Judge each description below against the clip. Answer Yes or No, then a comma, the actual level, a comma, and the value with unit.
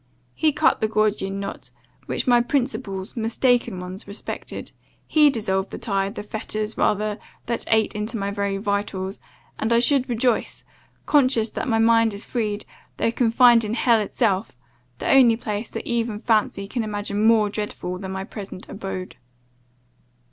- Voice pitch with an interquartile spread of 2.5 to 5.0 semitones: Yes, average, 2.8 semitones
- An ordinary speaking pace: Yes, average, 155 wpm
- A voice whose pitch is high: Yes, high, 215 Hz